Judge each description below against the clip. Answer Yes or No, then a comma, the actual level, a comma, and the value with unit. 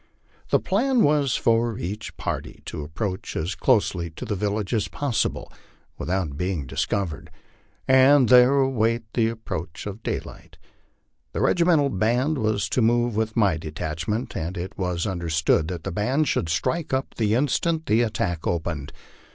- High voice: No, low, 110 Hz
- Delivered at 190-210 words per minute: No, average, 155 wpm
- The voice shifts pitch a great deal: Yes, wide, 6.5 semitones